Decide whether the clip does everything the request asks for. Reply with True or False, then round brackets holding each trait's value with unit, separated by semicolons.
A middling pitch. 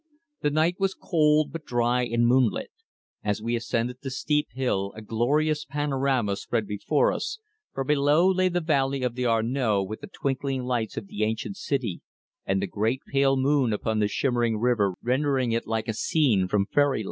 False (125 Hz)